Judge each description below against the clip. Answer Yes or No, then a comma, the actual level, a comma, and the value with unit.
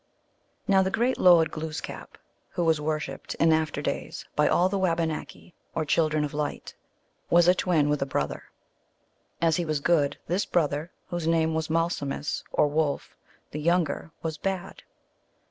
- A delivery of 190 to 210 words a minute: No, average, 160 wpm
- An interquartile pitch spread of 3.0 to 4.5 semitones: No, narrow, 2.4 semitones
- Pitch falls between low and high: Yes, medium, 160 Hz